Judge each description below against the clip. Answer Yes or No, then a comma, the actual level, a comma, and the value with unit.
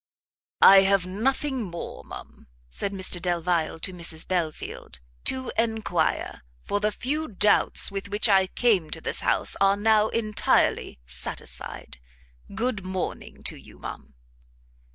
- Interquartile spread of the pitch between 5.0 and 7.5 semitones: No, average, 3.7 semitones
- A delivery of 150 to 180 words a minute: No, slow, 135 wpm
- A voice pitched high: Yes, high, 195 Hz